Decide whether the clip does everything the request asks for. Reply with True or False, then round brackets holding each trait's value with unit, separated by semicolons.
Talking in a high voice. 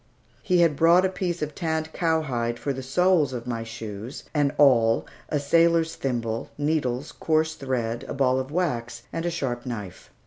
False (140 Hz)